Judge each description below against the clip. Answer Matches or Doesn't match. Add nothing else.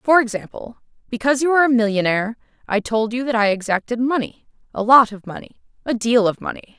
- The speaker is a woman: Matches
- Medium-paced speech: Matches